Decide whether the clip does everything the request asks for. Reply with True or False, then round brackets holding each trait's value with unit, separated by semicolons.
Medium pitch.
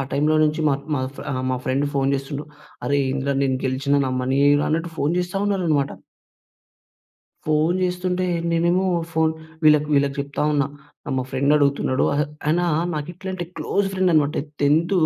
True (150 Hz)